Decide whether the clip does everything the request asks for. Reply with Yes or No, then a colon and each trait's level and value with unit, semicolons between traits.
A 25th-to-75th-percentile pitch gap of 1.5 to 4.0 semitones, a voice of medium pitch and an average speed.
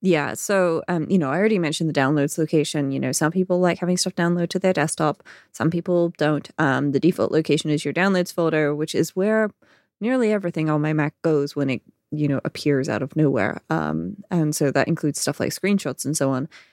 No: average, 3.6 semitones; medium, 155 Hz; fast, 220 wpm